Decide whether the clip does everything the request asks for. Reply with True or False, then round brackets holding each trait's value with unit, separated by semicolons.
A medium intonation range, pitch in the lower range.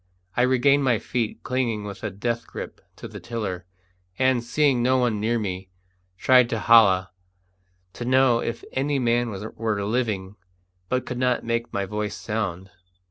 True (3.3 semitones; 115 Hz)